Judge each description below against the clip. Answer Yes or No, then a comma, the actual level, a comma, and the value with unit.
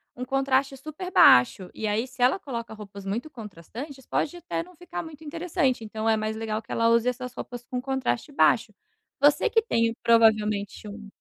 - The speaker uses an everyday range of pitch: Yes, average, 4.5 semitones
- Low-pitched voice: No, high, 245 Hz